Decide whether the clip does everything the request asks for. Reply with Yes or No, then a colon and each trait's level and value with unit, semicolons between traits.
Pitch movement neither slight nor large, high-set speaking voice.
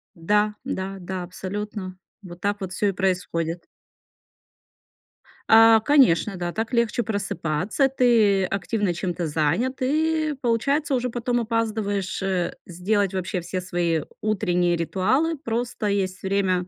Yes: average, 4.2 semitones; high, 200 Hz